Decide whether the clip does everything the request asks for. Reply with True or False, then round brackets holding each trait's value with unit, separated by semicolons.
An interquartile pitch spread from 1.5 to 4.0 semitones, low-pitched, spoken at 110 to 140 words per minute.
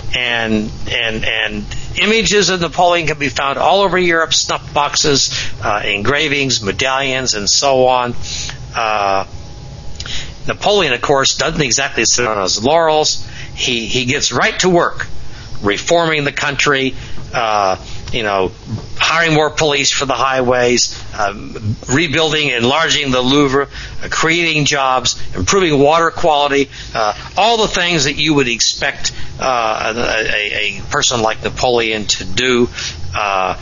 False (4.8 semitones; 130 Hz; 135 wpm)